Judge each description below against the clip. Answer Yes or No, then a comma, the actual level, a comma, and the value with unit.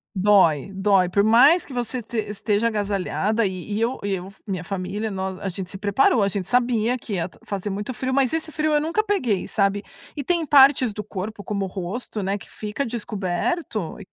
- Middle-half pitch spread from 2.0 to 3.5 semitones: No, average, 4.2 semitones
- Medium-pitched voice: No, high, 210 Hz